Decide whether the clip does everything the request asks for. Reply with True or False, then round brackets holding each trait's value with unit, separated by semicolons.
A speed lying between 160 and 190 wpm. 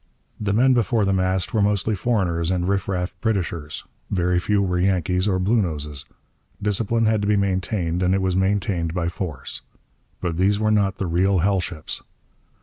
True (175 wpm)